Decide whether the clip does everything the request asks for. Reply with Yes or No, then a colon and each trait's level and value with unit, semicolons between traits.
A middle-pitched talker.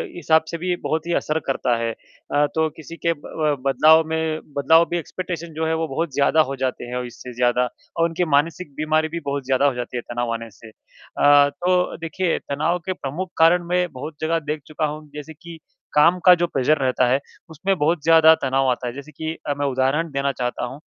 Yes: medium, 155 Hz